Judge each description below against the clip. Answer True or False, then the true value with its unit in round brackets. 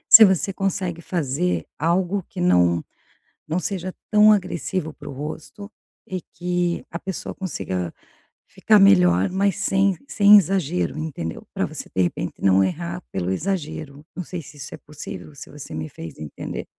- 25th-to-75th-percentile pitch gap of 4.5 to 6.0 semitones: True (5.6 semitones)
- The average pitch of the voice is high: False (170 Hz)